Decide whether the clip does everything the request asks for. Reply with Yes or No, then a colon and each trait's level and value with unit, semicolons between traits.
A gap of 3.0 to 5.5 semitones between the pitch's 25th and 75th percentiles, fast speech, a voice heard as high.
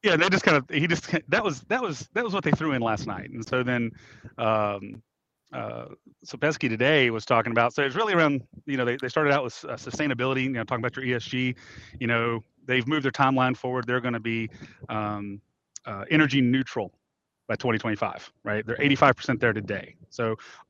No: average, 3.4 semitones; fast, 210 wpm; low, 125 Hz